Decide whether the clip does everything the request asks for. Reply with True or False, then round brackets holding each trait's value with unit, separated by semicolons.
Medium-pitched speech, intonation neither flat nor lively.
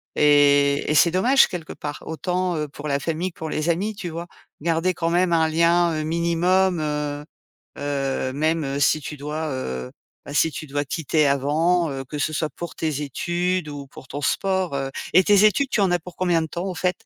True (160 Hz; 3.4 semitones)